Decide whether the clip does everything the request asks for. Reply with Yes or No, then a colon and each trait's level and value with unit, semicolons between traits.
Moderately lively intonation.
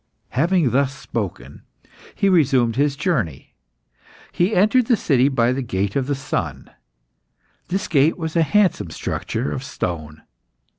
No: wide, 6.3 semitones